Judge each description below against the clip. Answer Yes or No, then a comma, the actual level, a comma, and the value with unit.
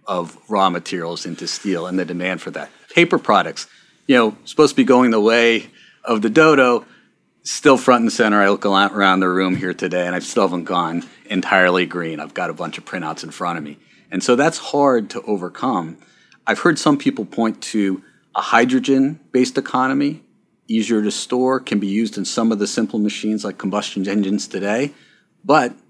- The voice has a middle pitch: No, low, 105 Hz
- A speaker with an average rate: Yes, average, 195 wpm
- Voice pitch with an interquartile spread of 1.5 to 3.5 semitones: No, average, 5.1 semitones